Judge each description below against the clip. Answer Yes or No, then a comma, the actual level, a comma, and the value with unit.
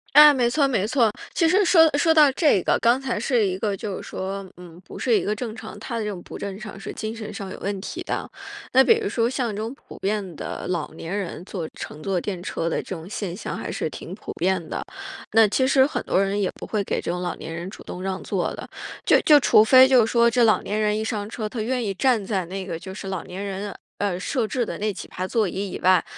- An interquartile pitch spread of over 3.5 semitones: Yes, average, 4.2 semitones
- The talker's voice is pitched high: Yes, high, 210 Hz